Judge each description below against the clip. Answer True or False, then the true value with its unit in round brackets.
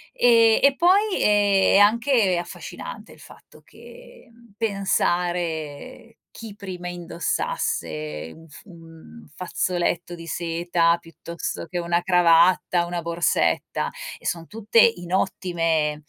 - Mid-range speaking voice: True (175 Hz)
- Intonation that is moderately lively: True (3.7 semitones)